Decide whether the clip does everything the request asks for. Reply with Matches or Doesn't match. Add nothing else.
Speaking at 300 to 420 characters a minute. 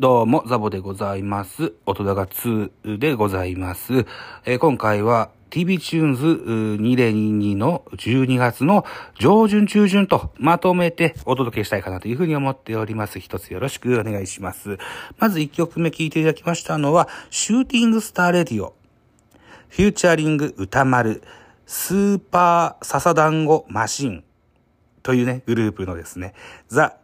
Matches